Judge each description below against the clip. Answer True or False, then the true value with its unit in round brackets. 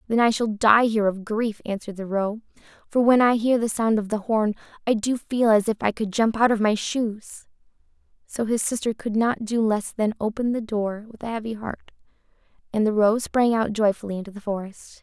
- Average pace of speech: False (220 wpm)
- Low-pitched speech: False (220 Hz)